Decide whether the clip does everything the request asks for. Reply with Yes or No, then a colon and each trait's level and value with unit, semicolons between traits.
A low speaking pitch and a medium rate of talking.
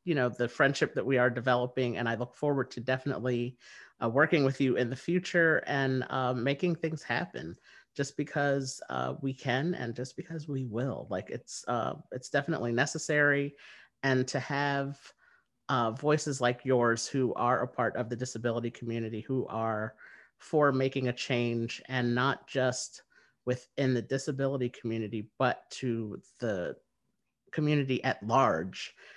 Yes: low, 130 Hz; average, 155 wpm